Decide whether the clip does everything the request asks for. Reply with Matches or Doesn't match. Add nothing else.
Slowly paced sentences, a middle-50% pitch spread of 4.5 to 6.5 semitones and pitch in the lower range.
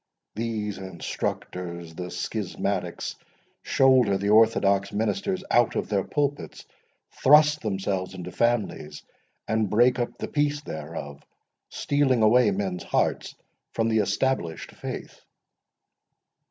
Matches